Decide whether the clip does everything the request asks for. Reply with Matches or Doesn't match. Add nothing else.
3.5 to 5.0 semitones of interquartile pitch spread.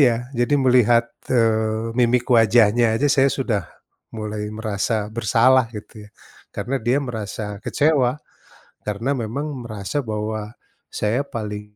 Doesn't match